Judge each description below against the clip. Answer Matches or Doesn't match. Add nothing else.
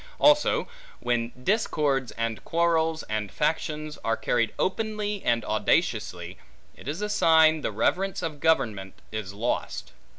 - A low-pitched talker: Doesn't match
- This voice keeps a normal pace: Doesn't match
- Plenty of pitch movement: Matches